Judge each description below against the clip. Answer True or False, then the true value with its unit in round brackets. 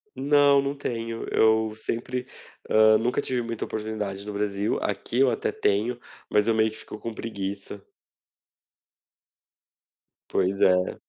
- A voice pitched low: True (110 Hz)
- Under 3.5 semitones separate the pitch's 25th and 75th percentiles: True (2.8 semitones)